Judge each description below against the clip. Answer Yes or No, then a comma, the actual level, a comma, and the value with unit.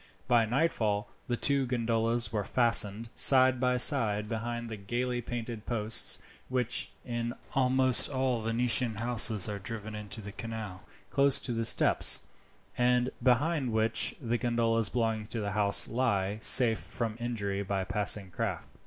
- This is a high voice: No, low, 115 Hz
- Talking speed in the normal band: Yes, average, 145 wpm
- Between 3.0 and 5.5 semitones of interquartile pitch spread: No, narrow, 2.5 semitones